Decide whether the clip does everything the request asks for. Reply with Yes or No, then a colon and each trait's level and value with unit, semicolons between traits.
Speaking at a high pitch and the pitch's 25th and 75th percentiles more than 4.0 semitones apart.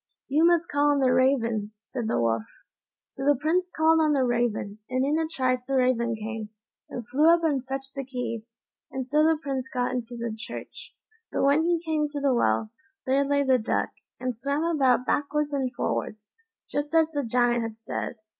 No: very high, 265 Hz; average, 3.6 semitones